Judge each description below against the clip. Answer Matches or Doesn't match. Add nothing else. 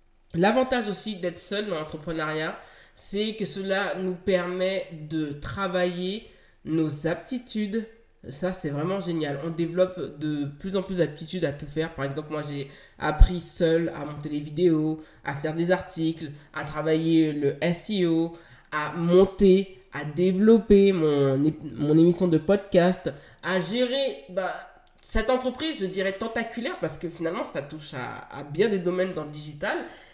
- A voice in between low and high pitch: Matches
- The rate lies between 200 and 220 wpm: Doesn't match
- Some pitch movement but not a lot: Matches